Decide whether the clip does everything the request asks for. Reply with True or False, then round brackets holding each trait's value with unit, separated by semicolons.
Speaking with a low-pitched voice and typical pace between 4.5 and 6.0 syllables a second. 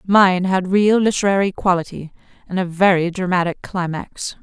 False (185 Hz; 4.8 syllables/s)